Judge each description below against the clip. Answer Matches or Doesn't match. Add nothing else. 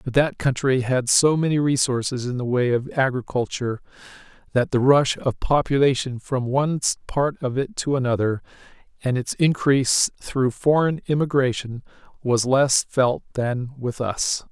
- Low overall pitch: Matches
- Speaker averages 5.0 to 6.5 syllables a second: Doesn't match